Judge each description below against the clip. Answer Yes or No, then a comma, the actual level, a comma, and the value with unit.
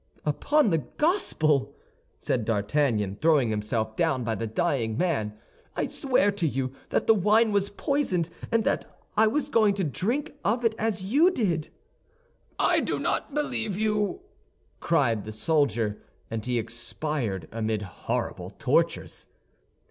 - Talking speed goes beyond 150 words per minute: No, average, 140 wpm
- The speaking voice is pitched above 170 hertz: No, medium, 155 Hz